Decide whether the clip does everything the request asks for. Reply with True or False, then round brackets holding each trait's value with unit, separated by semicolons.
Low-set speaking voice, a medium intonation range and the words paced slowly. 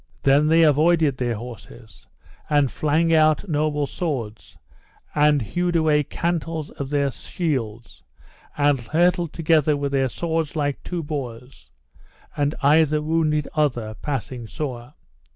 False (150 Hz; 3.2 semitones; 125 wpm)